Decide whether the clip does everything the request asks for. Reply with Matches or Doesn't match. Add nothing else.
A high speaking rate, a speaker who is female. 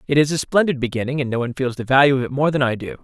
Doesn't match